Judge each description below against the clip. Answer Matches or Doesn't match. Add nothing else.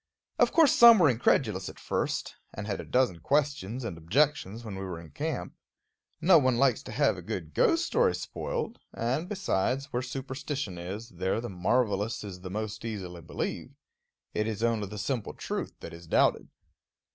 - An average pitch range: Doesn't match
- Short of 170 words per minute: Doesn't match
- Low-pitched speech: Matches